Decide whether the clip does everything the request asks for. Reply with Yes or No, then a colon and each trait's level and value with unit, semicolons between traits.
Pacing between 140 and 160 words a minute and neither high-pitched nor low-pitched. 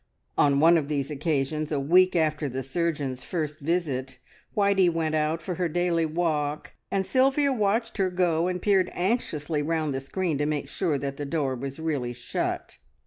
No: average, 180 wpm; medium, 160 Hz